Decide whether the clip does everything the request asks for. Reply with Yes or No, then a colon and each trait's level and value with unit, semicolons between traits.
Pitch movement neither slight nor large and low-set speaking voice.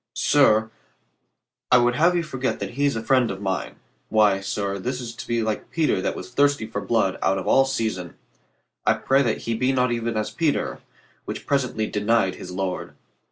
Yes: average, 4.3 semitones; low, 115 Hz